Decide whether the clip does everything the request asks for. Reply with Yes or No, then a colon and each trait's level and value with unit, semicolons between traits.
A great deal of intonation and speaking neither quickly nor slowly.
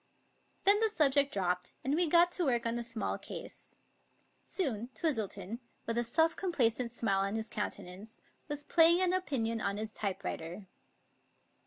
Yes: wide, 7.3 semitones; average, 155 wpm